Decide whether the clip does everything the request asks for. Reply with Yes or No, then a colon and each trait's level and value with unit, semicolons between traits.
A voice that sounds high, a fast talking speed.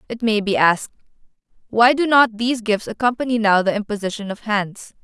No: high, 220 Hz; average, 180 wpm